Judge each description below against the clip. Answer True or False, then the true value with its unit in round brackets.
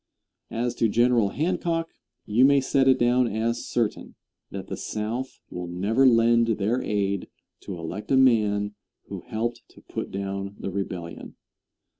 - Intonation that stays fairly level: False (3.8 semitones)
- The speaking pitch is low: True (115 Hz)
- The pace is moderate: True (150 wpm)